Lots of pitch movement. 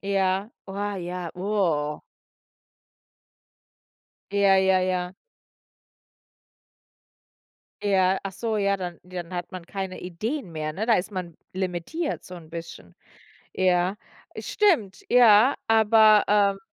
No: narrow, 2.6 semitones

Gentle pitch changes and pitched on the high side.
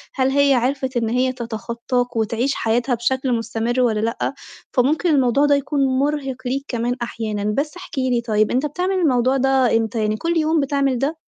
No: average, 3.0 semitones; very high, 255 Hz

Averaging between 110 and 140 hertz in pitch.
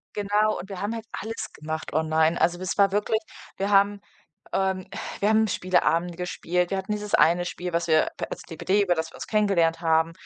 No: medium, 185 Hz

